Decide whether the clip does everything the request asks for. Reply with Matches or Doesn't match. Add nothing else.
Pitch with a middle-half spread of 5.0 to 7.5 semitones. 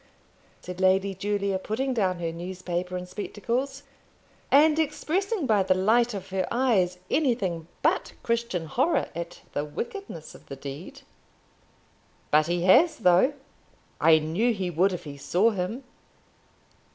Matches